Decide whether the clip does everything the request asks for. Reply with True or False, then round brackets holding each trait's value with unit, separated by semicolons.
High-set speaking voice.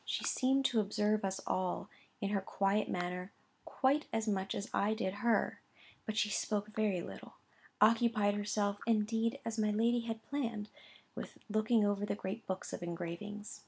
True (210 Hz)